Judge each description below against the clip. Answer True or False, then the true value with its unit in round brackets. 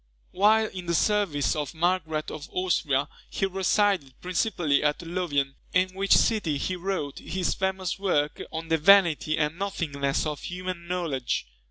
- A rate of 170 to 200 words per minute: False (150 wpm)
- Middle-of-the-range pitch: True (175 Hz)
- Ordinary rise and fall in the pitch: True (4.1 semitones)